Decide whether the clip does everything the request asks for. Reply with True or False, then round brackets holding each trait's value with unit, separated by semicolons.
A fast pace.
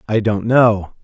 False (175 wpm)